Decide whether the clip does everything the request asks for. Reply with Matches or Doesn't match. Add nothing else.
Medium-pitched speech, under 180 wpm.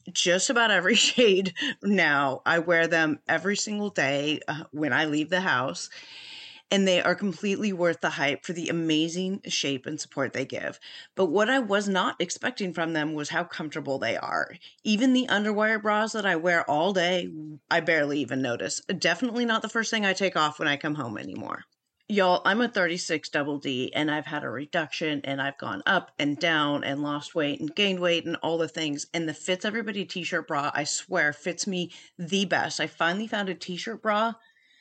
Doesn't match